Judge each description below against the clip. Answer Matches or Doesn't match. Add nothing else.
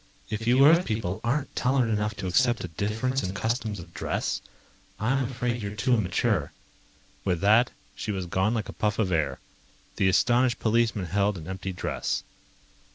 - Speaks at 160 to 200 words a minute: Matches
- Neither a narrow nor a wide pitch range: Matches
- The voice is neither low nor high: Doesn't match